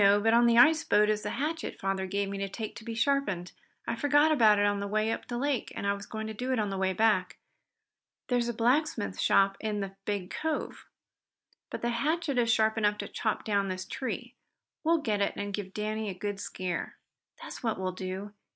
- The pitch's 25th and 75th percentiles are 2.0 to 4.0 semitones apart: Yes, average, 3.3 semitones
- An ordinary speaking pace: No, fast, 225 wpm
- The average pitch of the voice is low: No, high, 215 Hz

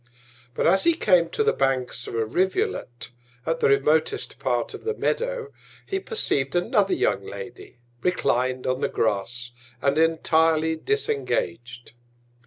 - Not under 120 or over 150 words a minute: Yes, average, 140 wpm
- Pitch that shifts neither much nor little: No, wide, 8.1 semitones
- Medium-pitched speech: Yes, medium, 160 Hz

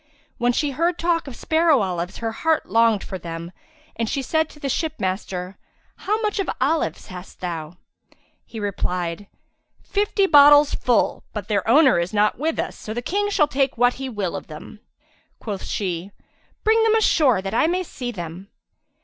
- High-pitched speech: Yes, high, 240 Hz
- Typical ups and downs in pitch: No, wide, 8.7 semitones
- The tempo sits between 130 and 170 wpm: No, average, 180 wpm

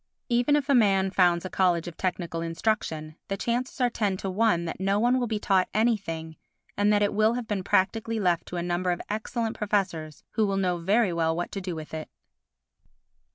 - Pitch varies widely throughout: No, average, 4.0 semitones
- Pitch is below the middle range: No, high, 195 Hz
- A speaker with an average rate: No, fast, 210 wpm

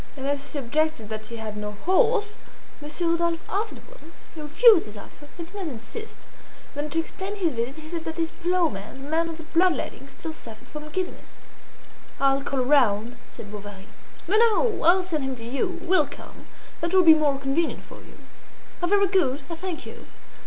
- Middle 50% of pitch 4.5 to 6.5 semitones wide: Yes, average, 5.3 semitones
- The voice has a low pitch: No, very high, 315 Hz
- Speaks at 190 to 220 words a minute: Yes, average, 200 wpm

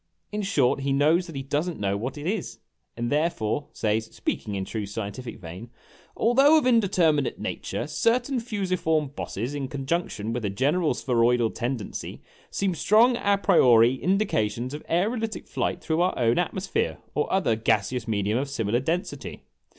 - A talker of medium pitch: Yes, medium, 145 Hz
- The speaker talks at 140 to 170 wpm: Yes, average, 165 wpm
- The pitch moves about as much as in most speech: No, wide, 7.9 semitones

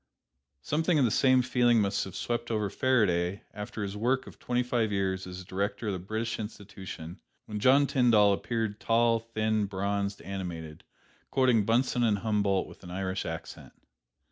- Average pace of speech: Yes, average, 165 wpm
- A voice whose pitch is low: Yes, low, 105 Hz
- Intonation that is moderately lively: Yes, average, 3.4 semitones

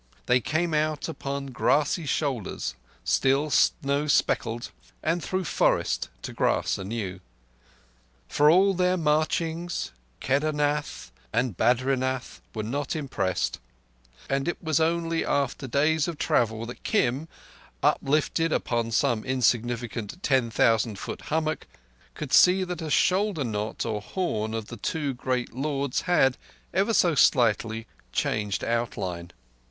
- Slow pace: Yes, slow, 120 wpm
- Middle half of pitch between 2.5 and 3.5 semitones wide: No, average, 5.3 semitones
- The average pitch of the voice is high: No, low, 135 Hz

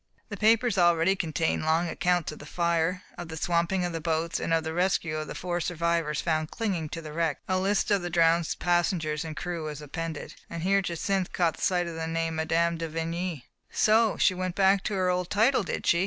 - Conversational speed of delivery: No, fast, 225 wpm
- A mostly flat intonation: Yes, narrow, 2.2 semitones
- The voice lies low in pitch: No, medium, 170 Hz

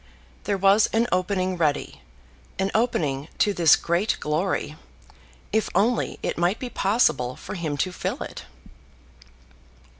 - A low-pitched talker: No, medium, 185 Hz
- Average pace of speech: No, slow, 130 wpm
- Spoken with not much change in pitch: No, average, 4.8 semitones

